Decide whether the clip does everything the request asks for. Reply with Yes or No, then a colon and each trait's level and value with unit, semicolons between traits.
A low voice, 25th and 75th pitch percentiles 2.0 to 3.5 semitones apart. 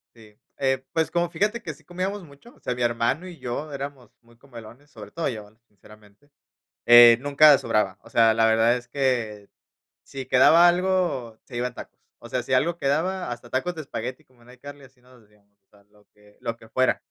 No: low, 125 Hz; average, 4.2 semitones